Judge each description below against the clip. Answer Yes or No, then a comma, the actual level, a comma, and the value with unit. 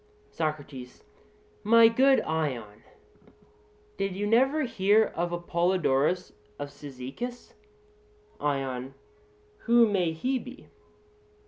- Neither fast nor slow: No, slow, 90 wpm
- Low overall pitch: No, medium, 175 Hz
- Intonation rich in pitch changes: Yes, wide, 8.3 semitones